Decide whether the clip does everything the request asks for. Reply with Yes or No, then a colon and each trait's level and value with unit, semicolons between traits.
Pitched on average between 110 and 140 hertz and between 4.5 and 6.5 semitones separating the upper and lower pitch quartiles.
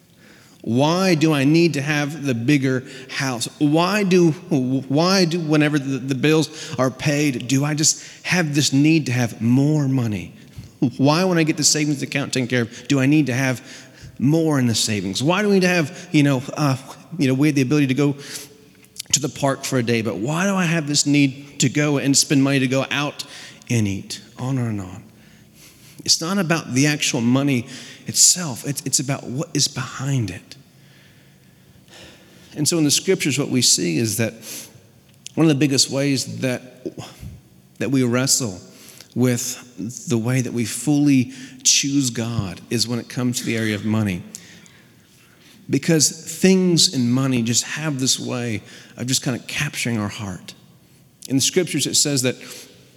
No: low, 135 Hz; average, 3.3 semitones